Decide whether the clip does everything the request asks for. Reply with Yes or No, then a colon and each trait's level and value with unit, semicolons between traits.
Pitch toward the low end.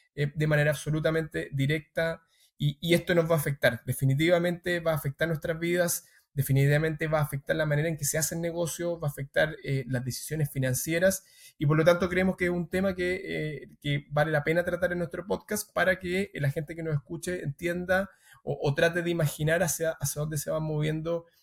No: medium, 160 Hz